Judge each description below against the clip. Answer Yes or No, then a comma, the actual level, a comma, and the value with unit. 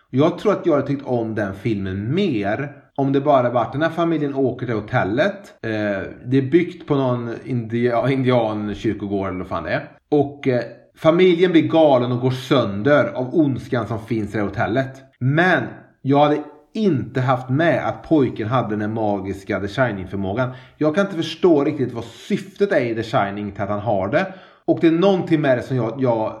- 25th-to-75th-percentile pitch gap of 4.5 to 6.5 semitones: Yes, average, 4.9 semitones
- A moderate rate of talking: No, fast, 200 wpm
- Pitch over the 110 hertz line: Yes, low, 130 Hz